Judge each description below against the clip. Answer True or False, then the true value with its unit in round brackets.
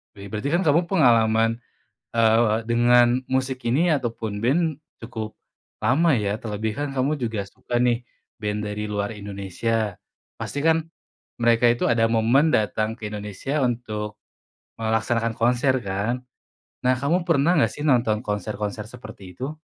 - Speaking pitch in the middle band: False (115 Hz)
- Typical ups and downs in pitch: True (3.4 semitones)